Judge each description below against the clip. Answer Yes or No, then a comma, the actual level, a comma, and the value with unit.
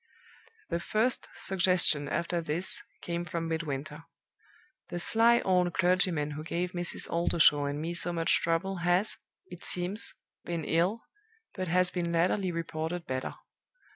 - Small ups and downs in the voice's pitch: Yes, narrow, 1.9 semitones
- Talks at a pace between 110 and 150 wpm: Yes, average, 140 wpm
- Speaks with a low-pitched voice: No, medium, 175 Hz